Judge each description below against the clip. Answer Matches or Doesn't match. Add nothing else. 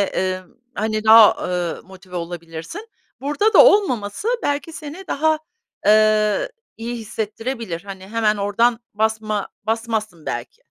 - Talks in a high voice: Matches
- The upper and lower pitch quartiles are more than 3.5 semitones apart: Matches